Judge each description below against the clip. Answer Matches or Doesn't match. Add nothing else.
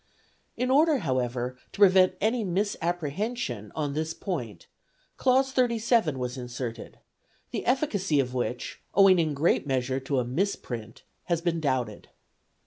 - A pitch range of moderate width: Doesn't match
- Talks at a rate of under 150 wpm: Matches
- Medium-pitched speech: Matches